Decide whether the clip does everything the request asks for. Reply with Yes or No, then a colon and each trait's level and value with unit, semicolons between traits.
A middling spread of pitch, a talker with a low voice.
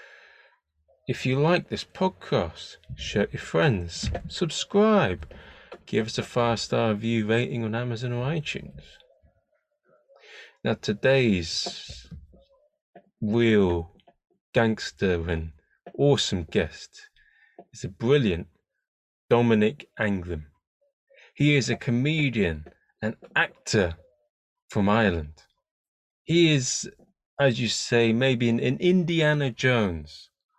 No: wide, 7.5 semitones; low, 120 Hz